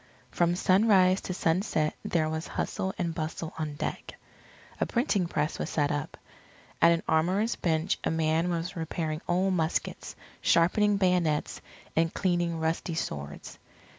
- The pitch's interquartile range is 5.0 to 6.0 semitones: No, narrow, 2.5 semitones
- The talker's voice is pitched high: No, medium, 170 Hz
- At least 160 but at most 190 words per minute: No, average, 140 wpm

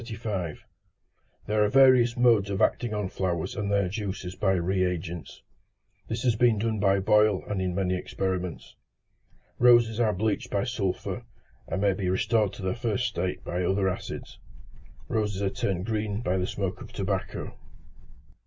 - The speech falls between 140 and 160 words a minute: Yes, average, 155 wpm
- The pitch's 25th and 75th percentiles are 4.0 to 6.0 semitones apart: No, average, 2.9 semitones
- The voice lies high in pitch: No, low, 100 Hz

